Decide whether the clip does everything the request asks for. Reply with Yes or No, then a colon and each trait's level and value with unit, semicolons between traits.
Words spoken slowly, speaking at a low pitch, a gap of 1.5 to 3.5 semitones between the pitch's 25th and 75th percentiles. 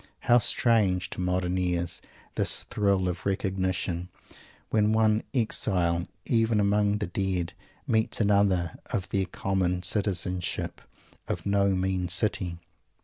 Yes: slow, 120 wpm; very low, 95 Hz; narrow, 2.5 semitones